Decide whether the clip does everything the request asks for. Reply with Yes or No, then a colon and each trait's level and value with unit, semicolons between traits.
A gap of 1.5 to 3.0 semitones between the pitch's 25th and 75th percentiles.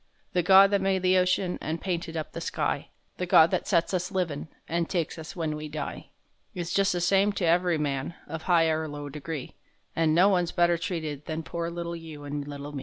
Yes: narrow, 2.6 semitones